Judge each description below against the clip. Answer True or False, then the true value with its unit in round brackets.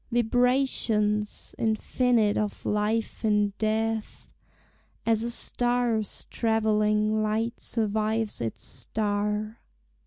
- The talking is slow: True (85 wpm)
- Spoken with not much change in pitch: True (1.3 semitones)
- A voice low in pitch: False (220 Hz)